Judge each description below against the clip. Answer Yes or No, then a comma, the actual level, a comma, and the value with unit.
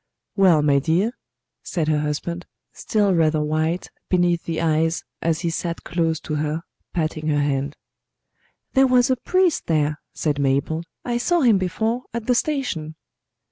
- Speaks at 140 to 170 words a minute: Yes, average, 155 wpm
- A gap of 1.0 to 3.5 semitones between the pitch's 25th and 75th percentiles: No, average, 4.8 semitones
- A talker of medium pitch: Yes, medium, 165 Hz